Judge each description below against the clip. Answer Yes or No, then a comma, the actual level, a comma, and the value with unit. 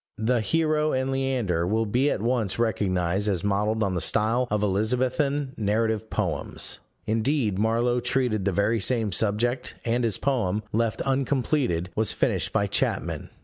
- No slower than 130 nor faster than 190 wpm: Yes, average, 150 wpm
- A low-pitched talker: Yes, low, 110 Hz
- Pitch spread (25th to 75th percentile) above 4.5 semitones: No, average, 3.8 semitones